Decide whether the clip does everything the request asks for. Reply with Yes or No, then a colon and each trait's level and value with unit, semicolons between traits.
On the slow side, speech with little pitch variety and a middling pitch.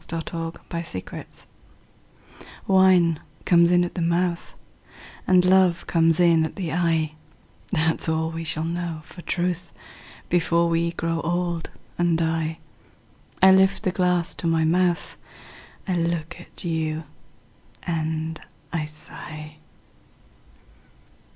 Yes: slow, 120 wpm; narrow, 1.6 semitones; medium, 170 Hz